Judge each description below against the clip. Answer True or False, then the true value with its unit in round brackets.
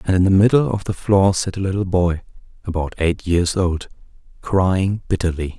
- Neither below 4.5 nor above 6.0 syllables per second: True (4.9 syllables/s)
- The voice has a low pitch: True (95 Hz)